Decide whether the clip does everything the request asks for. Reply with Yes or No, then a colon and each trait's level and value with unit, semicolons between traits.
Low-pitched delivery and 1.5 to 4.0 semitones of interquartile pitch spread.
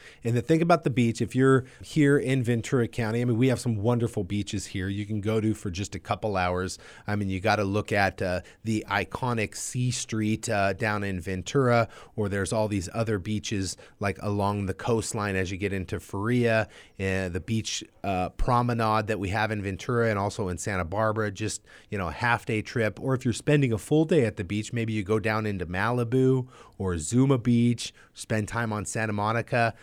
Yes: low, 110 Hz; average, 2.9 semitones